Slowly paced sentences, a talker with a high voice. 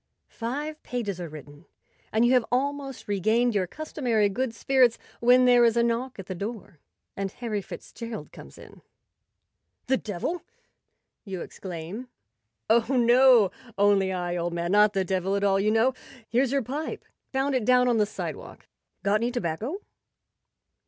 No: average, 165 wpm; high, 225 Hz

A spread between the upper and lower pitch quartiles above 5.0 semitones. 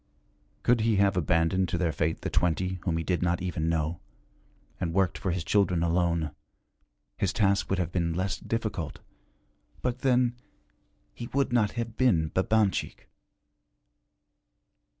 No: average, 4.3 semitones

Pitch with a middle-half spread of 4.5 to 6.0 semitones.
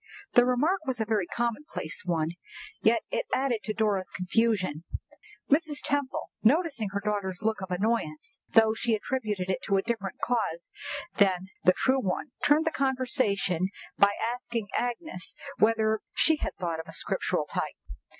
Yes: average, 5.3 semitones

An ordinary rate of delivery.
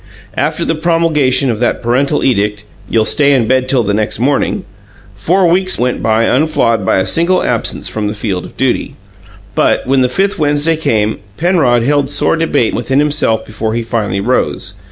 Yes: average, 180 wpm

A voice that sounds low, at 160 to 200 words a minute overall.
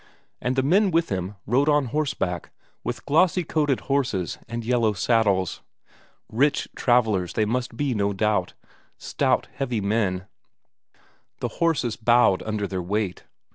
No: low, 115 Hz; slow, 135 wpm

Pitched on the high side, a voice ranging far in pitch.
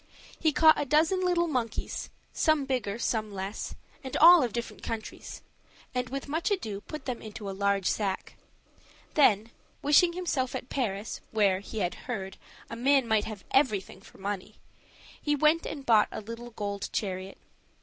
Yes: high, 235 Hz; wide, 6.3 semitones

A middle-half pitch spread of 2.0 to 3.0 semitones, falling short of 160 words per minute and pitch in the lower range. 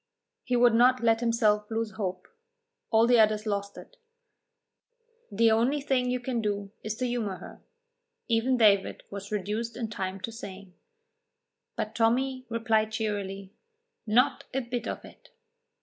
No: average, 2.7 semitones; average, 150 wpm; high, 225 Hz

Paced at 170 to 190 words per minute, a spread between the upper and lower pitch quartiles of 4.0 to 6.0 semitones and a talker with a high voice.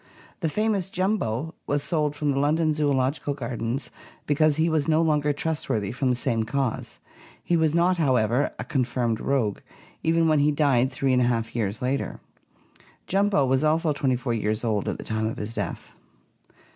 No: average, 185 wpm; average, 4.6 semitones; medium, 140 Hz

